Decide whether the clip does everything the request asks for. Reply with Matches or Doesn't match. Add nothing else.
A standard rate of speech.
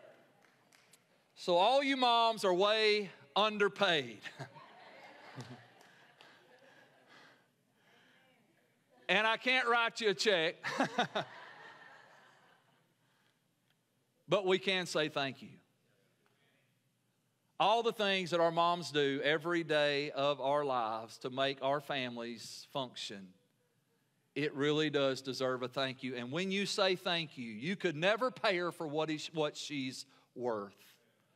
Doesn't match